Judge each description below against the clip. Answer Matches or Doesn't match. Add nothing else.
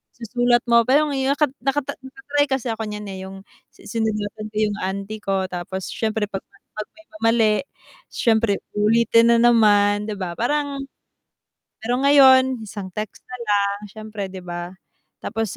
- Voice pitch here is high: Matches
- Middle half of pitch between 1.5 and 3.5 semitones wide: Matches